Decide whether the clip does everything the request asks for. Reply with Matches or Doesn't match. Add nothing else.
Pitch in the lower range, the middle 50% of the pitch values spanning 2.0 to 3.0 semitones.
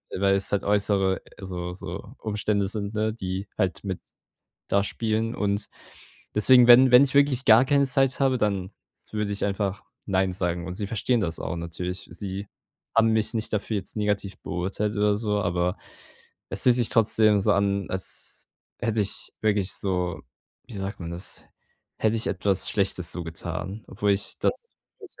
Matches